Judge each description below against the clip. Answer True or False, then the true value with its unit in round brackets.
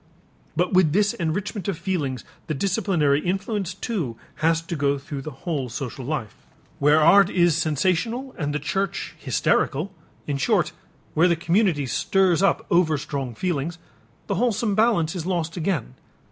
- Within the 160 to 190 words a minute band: False (150 wpm)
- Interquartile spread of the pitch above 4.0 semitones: True (4.8 semitones)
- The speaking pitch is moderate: True (165 Hz)